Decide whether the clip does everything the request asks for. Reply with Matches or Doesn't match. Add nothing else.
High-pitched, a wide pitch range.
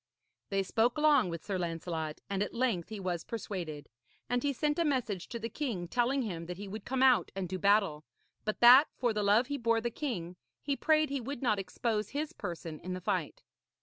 Matches